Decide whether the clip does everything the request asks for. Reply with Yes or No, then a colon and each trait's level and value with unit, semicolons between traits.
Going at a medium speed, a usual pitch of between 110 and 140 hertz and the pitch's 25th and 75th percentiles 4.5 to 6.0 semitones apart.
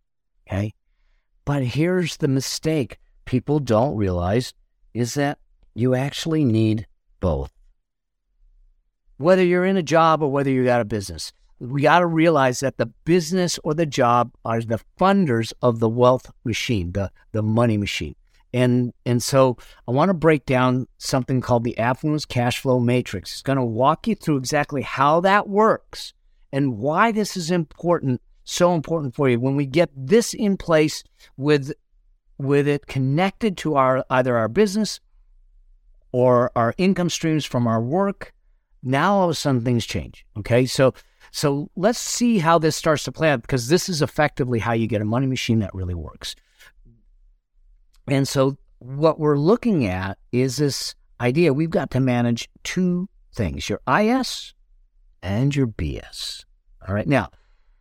Yes: average, 160 wpm; low, 135 Hz; average, 5.3 semitones